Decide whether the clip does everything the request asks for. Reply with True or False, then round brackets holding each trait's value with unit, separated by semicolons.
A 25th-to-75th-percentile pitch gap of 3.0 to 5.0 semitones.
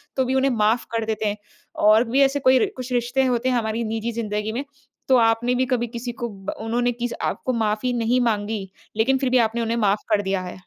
False (2.4 semitones)